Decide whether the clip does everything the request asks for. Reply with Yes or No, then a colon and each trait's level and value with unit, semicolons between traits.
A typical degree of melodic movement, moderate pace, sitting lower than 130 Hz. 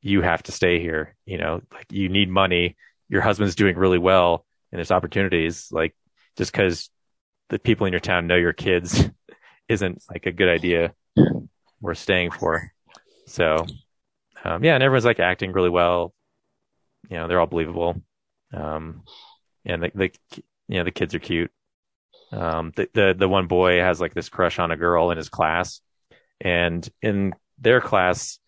No: narrow, 2.2 semitones; average, 175 wpm; very low, 90 Hz